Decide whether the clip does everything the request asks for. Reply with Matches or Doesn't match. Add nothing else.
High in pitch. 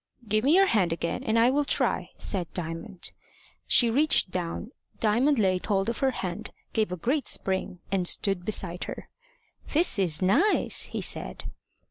Matches